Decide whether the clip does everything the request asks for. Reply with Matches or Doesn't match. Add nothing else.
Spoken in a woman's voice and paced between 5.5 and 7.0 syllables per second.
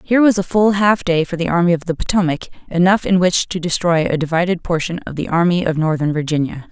Matches